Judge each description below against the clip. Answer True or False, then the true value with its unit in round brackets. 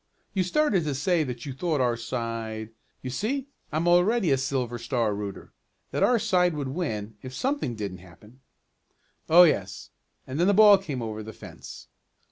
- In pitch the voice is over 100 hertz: True (135 Hz)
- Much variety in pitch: True (7.7 semitones)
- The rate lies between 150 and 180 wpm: True (175 wpm)